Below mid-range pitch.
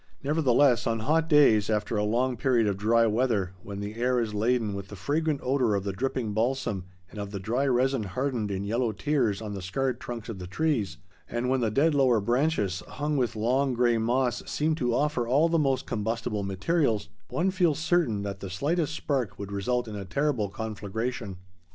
Yes: low, 120 Hz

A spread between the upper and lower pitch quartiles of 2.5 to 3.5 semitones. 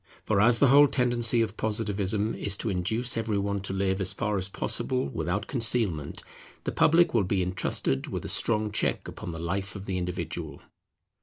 Yes: average, 3.2 semitones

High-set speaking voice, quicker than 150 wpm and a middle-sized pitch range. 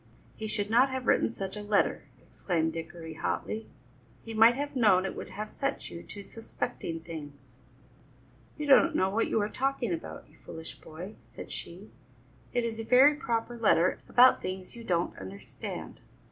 No: high, 210 Hz; average, 175 wpm; wide, 5.9 semitones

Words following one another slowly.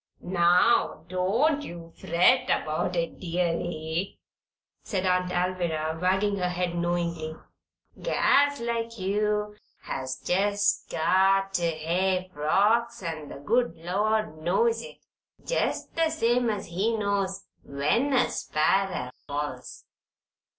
Yes: slow, 115 wpm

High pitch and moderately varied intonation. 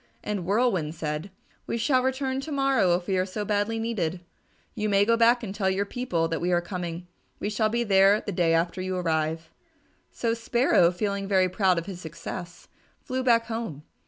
Yes: high, 195 Hz; average, 4.7 semitones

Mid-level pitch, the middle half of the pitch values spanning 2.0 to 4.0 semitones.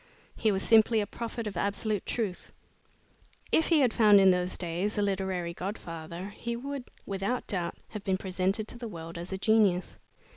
No: high, 200 Hz; average, 3.4 semitones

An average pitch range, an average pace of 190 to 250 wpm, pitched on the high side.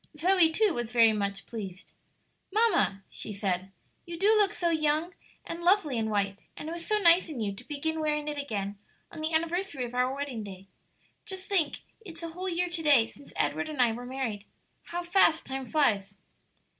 No: wide, 7.4 semitones; average, 195 wpm; very high, 295 Hz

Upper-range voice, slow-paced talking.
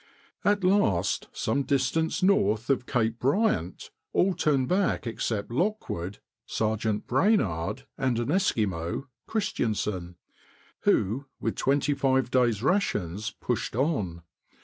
No: low, 125 Hz; slow, 110 wpm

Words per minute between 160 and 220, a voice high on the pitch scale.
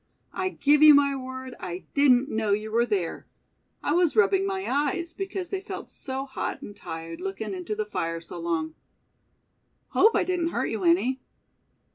Yes: average, 175 wpm; very high, 260 Hz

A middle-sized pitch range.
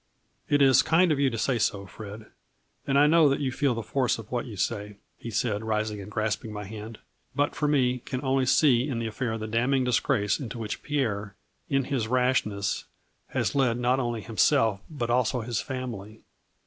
Yes: average, 3.7 semitones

